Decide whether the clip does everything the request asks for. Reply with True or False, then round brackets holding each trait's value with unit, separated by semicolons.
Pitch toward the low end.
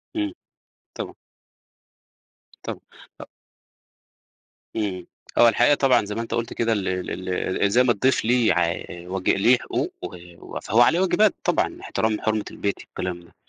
True (110 Hz)